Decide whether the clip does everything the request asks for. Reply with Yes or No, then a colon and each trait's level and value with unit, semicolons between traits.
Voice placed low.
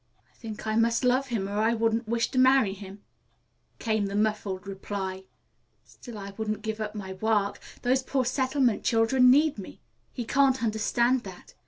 No: high, 220 Hz